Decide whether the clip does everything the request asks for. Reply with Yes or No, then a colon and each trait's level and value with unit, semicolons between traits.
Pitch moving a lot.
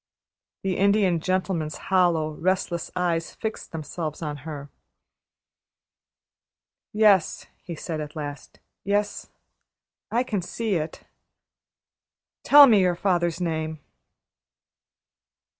No: average, 3.6 semitones